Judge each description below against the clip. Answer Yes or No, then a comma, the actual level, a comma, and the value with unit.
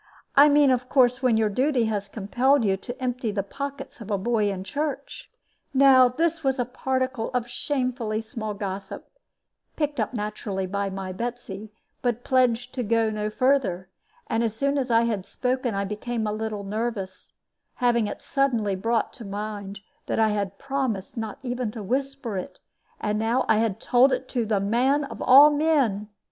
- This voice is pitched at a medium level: No, high, 230 Hz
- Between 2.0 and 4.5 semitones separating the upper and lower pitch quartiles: Yes, average, 3.8 semitones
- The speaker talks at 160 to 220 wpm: Yes, average, 180 wpm